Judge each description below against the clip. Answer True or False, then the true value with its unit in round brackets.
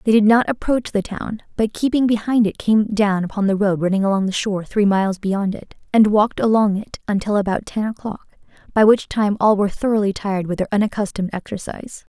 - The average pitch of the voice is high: True (205 Hz)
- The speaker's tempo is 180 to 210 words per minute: True (205 wpm)